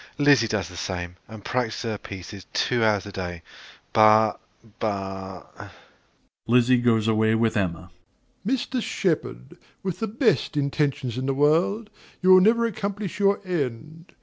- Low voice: Yes, low, 120 Hz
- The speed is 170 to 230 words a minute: No, average, 150 wpm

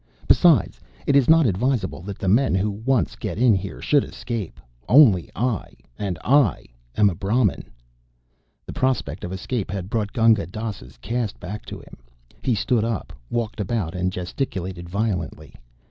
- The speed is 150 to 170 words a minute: Yes, average, 160 wpm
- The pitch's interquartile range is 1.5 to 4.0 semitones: No, average, 4.5 semitones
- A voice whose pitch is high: No, low, 105 Hz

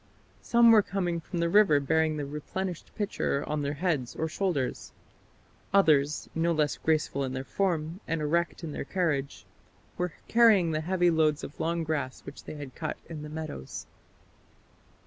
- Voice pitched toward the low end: No, medium, 160 Hz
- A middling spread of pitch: Yes, average, 3.2 semitones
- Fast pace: No, average, 165 wpm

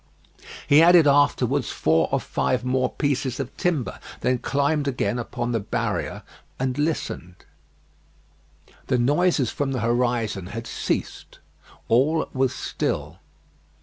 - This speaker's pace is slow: Yes, slow, 120 wpm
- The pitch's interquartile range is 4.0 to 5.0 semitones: No, average, 3.2 semitones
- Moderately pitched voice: No, low, 130 Hz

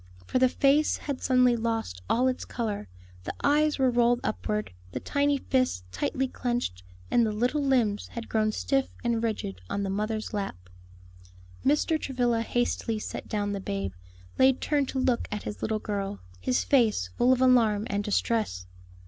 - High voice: Yes, high, 230 Hz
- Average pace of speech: Yes, average, 170 wpm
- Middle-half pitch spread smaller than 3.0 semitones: No, average, 4.0 semitones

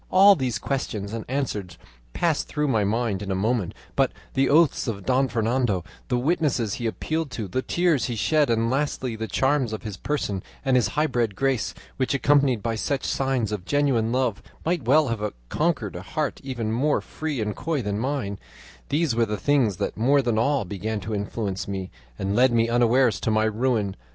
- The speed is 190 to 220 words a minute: Yes, average, 195 wpm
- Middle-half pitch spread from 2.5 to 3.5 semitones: No, average, 4.5 semitones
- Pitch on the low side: Yes, low, 120 Hz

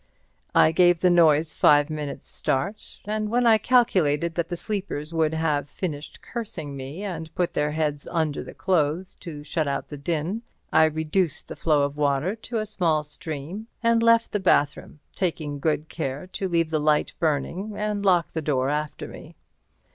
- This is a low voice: No, medium, 160 Hz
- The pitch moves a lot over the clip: No, average, 4.3 semitones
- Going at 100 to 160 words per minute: No, average, 175 wpm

